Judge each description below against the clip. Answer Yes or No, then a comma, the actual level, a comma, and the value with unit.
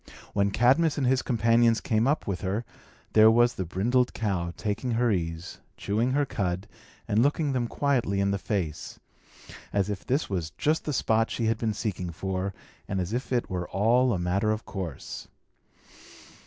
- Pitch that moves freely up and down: No, average, 4.2 semitones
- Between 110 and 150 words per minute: No, average, 180 wpm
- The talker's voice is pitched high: No, low, 110 Hz